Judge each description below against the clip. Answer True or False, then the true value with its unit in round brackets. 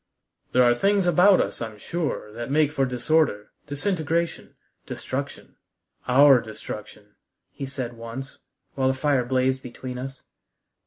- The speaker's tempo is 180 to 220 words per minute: False (135 wpm)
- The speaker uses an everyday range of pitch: True (3.9 semitones)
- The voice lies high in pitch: False (130 Hz)